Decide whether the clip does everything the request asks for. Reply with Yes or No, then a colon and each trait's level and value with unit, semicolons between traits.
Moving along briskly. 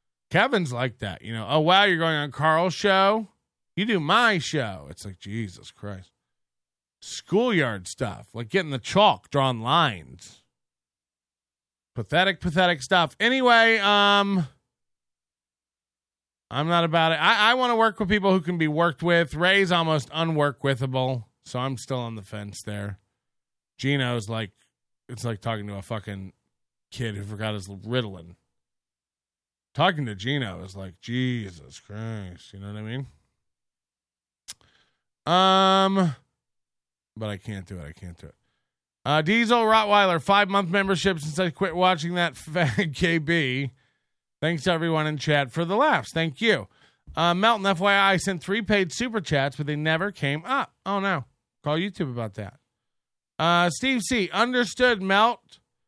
No: average, 150 wpm